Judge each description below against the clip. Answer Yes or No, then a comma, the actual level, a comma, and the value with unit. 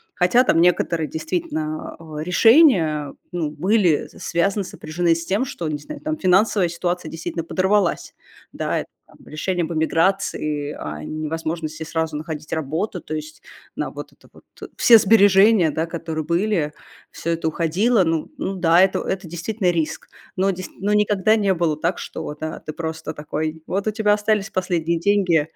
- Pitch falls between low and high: Yes, medium, 170 Hz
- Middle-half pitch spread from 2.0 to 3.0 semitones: No, average, 3.7 semitones